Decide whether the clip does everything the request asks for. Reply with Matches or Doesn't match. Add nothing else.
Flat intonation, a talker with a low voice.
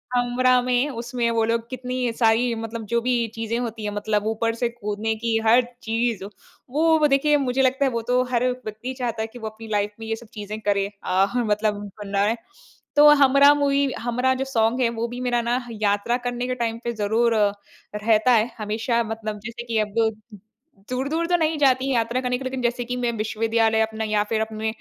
Doesn't match